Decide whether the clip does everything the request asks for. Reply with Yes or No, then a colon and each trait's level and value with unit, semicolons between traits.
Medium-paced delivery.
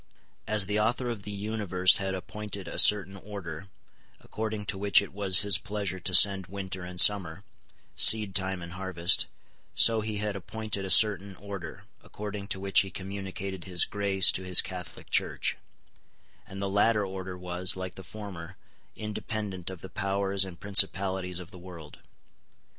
Yes: average, 160 wpm